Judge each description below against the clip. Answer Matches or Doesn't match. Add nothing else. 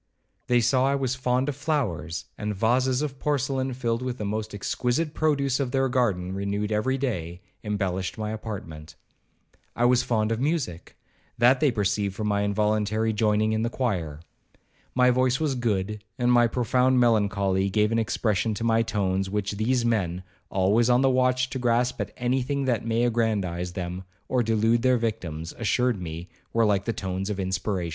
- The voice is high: Doesn't match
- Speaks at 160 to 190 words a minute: Matches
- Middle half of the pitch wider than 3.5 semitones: Matches